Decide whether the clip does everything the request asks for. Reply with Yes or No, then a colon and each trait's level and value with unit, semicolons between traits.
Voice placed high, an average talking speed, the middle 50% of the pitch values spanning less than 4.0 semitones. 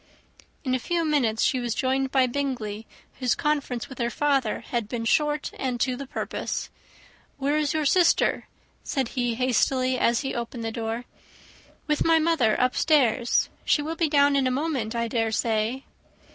Yes: very high, 260 Hz; average, 170 wpm; average, 3.6 semitones